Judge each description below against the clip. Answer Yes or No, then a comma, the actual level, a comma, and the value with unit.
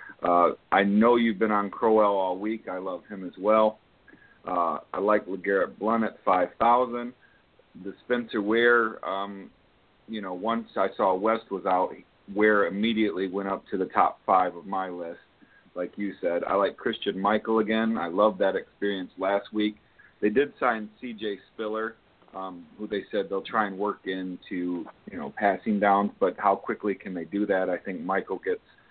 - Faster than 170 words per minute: Yes, average, 180 wpm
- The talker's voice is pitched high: No, low, 105 Hz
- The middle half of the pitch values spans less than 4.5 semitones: Yes, narrow, 2.4 semitones